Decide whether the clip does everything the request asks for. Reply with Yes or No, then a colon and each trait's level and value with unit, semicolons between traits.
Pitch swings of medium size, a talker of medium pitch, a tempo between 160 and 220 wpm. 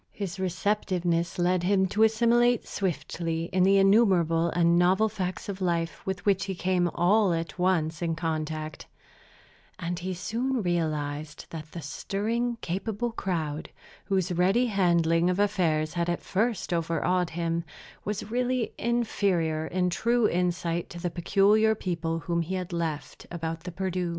No: average, 3.1 semitones; medium, 180 Hz; average, 145 wpm